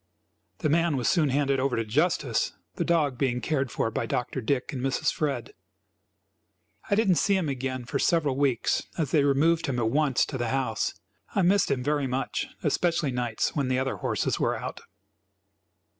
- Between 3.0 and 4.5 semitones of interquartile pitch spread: Yes, average, 3.6 semitones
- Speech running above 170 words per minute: Yes, average, 190 wpm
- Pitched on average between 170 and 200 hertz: No, medium, 140 Hz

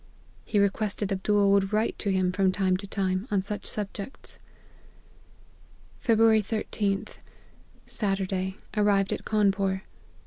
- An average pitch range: No, narrow, 1.6 semitones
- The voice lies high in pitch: Yes, high, 200 Hz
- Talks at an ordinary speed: No, slow, 125 wpm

